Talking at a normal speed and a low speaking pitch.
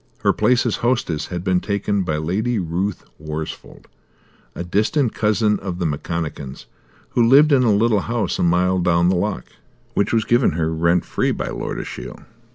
Yes: average, 175 wpm; very low, 95 Hz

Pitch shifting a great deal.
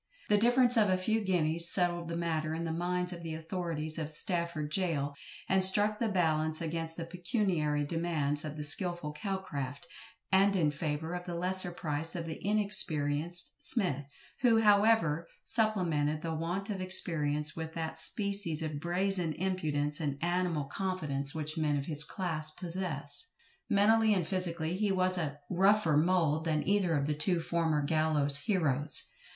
No: average, 3.5 semitones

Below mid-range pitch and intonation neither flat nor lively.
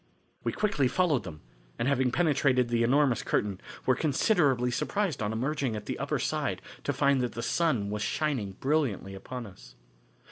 Yes: low, 125 Hz; average, 5.0 semitones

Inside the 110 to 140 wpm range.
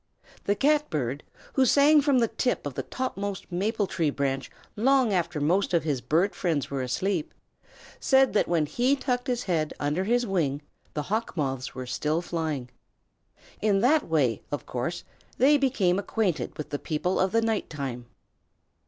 No: average, 170 wpm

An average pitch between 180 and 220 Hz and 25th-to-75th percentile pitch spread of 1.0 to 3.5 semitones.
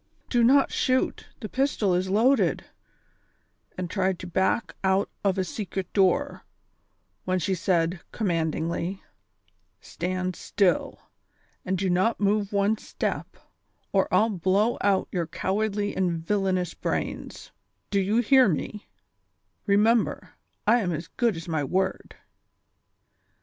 Yes: high, 190 Hz; average, 2.8 semitones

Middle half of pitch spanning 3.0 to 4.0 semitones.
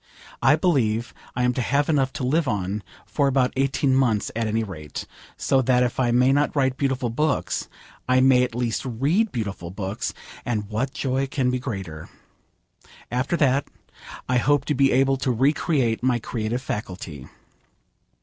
Yes: average, 3.3 semitones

